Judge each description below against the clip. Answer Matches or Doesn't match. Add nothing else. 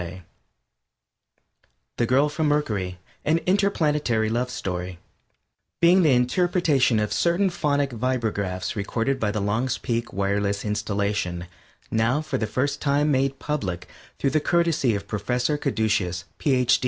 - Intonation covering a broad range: Matches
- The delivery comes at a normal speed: Doesn't match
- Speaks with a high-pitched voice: Doesn't match